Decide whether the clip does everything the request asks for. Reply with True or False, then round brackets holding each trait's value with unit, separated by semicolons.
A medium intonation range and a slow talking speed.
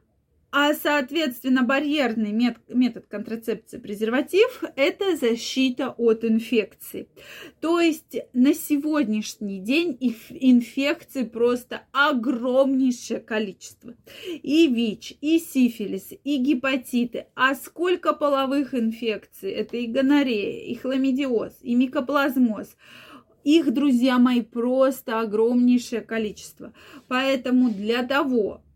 True (3.8 semitones; 95 wpm)